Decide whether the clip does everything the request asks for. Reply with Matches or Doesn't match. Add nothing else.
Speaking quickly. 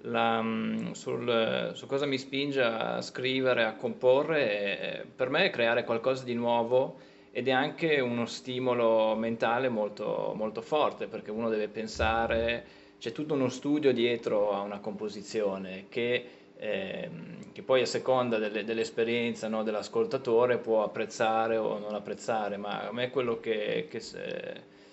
Doesn't match